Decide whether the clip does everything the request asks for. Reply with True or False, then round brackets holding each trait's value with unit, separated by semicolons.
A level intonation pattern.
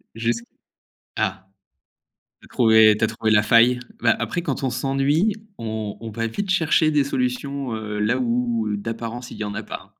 False (3.5 semitones)